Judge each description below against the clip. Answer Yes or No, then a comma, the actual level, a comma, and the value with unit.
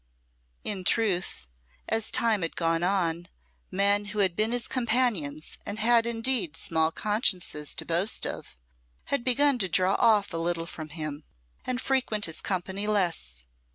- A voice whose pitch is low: No, high, 195 Hz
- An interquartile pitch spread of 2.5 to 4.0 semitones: No, average, 5.3 semitones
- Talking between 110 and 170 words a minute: Yes, average, 155 wpm